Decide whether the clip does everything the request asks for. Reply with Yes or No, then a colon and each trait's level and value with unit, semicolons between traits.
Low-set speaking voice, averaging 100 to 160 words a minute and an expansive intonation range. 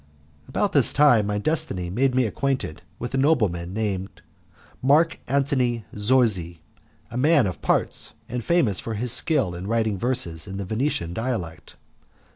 Yes: low, 115 Hz; average, 150 wpm; wide, 5.7 semitones